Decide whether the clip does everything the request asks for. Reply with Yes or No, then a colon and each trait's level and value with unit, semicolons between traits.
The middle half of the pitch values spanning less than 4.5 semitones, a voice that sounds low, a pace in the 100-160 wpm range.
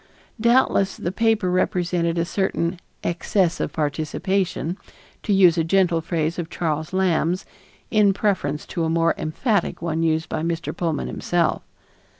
No: average, 2.7 semitones; medium, 170 Hz; average, 145 wpm